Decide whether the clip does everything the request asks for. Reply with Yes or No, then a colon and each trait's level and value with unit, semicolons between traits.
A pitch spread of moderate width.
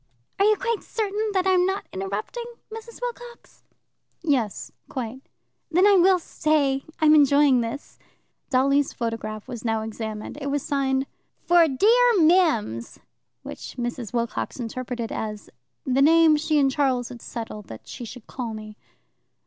No: wide, 7.0 semitones